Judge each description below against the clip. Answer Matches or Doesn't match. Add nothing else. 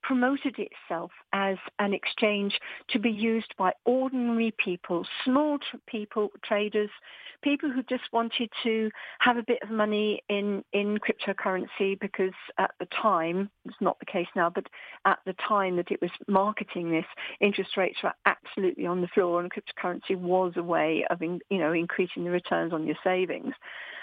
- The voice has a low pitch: Doesn't match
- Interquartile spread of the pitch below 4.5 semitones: Matches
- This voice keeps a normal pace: Matches